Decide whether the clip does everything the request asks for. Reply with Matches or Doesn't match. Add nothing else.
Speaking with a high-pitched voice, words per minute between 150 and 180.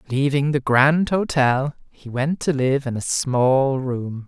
Doesn't match